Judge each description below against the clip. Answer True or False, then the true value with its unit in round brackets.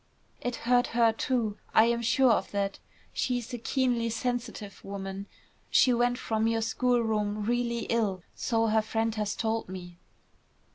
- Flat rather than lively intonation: True (2.3 semitones)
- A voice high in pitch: True (225 Hz)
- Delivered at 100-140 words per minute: False (155 wpm)